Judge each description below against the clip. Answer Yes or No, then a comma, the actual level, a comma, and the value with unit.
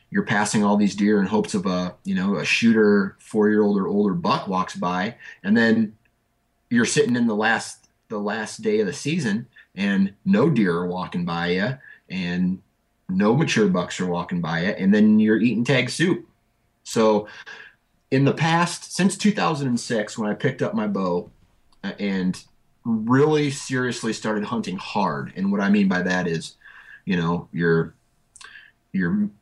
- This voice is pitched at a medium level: No, low, 115 Hz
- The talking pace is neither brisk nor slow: Yes, average, 170 wpm